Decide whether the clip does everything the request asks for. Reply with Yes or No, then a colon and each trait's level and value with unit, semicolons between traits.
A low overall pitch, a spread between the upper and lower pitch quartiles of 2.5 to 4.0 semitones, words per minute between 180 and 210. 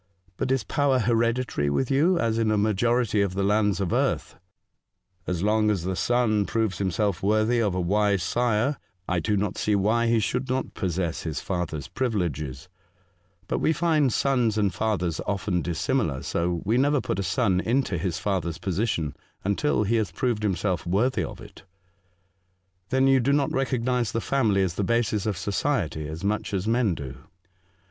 No: low, 105 Hz; average, 4.6 semitones; average, 185 wpm